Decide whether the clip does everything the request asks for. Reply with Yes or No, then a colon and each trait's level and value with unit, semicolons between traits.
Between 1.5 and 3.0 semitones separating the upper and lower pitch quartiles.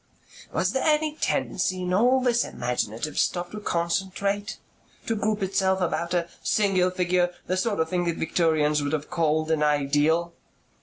No: average, 3.8 semitones